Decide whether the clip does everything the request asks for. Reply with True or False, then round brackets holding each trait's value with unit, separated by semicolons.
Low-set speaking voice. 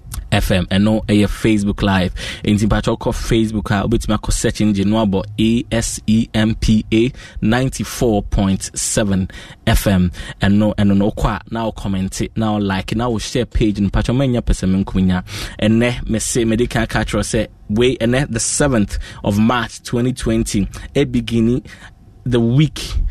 True (110 Hz)